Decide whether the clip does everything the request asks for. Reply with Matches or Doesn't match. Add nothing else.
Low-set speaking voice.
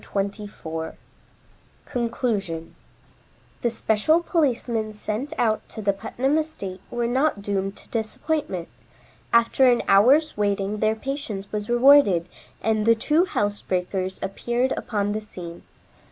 Doesn't match